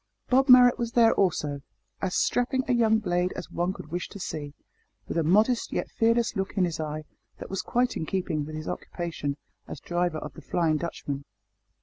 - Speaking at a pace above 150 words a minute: Yes, average, 200 wpm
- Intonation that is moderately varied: No, wide, 6.7 semitones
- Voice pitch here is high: No, medium, 180 Hz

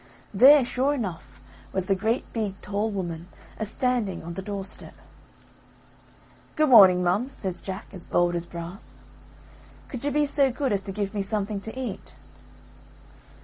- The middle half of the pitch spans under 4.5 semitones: No, average, 4.8 semitones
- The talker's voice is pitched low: No, high, 205 Hz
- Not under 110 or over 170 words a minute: Yes, average, 160 wpm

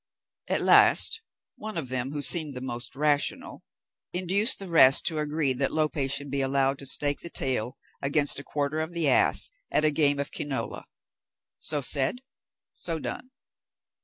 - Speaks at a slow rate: No, average, 165 wpm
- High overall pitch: No, medium, 145 Hz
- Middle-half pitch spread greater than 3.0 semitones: No, average, 2.7 semitones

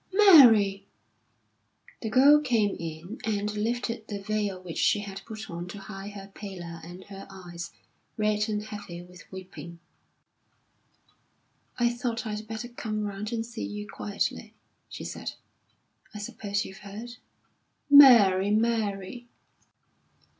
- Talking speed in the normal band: No, slow, 130 wpm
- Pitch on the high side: Yes, high, 210 Hz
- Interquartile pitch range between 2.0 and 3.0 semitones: Yes, average, 2.7 semitones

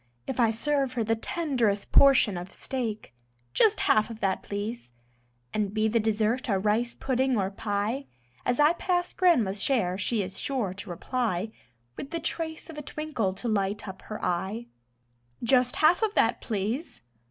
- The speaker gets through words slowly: No, average, 170 wpm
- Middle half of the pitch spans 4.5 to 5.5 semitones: Yes, average, 4.8 semitones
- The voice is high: Yes, high, 225 Hz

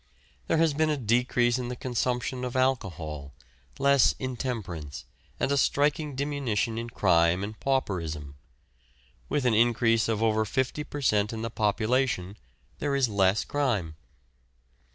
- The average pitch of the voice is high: No, low, 120 Hz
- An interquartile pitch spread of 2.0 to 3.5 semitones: No, average, 4.5 semitones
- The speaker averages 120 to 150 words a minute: Yes, average, 140 wpm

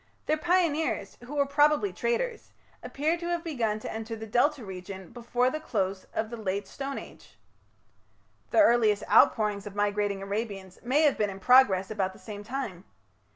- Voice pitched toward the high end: Yes, high, 225 Hz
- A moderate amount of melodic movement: No, wide, 6.5 semitones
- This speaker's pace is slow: No, average, 170 wpm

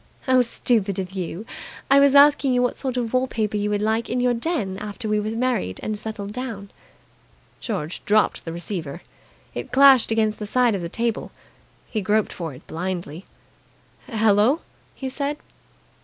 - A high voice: Yes, high, 215 Hz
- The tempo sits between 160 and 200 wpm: Yes, average, 170 wpm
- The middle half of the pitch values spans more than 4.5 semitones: No, average, 4.0 semitones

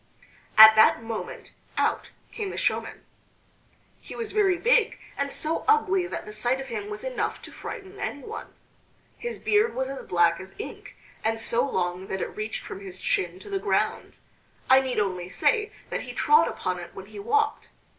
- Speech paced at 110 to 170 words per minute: No, average, 185 wpm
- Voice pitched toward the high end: Yes, very high, 260 Hz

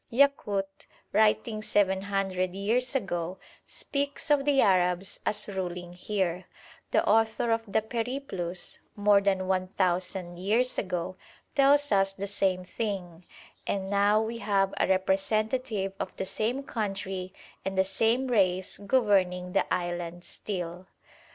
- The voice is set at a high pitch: Yes, high, 195 Hz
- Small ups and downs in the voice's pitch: No, average, 3.0 semitones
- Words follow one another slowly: Yes, slow, 130 wpm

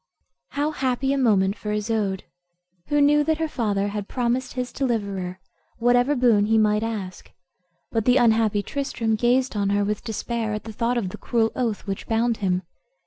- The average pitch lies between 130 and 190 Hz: No, high, 225 Hz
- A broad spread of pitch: No, average, 3.3 semitones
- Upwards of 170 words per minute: Yes, average, 180 wpm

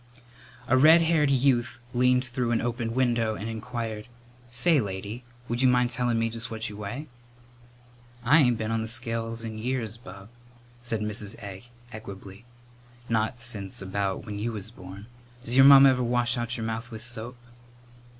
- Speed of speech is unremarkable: Yes, average, 170 wpm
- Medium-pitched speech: No, low, 115 Hz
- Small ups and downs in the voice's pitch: Yes, narrow, 2.2 semitones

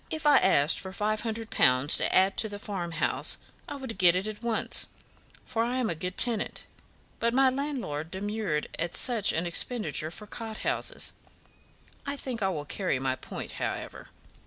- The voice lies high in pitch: Yes, high, 210 Hz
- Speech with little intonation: No, wide, 5.4 semitones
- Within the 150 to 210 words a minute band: Yes, average, 180 wpm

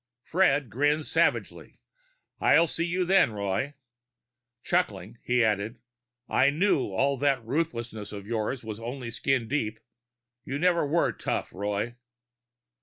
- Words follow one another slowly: Yes, slow, 125 wpm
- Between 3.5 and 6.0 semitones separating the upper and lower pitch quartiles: Yes, wide, 5.4 semitones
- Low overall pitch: Yes, low, 130 Hz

